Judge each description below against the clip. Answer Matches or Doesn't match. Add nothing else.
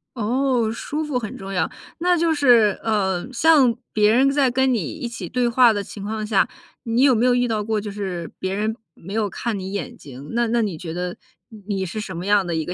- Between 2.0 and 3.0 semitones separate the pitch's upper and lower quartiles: Doesn't match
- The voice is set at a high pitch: Matches